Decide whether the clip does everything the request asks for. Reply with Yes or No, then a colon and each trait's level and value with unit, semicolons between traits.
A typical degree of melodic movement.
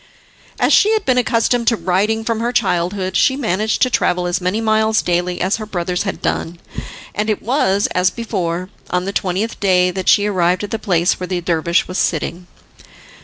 Yes: average, 3.6 semitones